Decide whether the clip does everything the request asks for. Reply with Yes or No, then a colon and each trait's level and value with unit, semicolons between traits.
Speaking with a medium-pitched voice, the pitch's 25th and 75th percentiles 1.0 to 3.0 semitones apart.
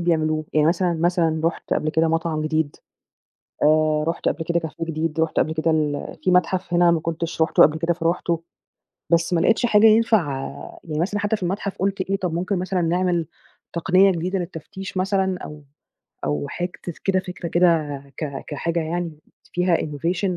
Yes: medium, 170 Hz; narrow, 2.6 semitones